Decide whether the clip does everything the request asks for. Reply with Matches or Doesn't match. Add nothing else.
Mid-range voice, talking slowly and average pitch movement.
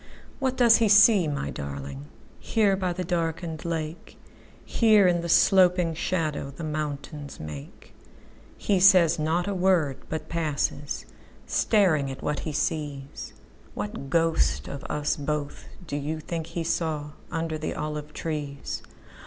Matches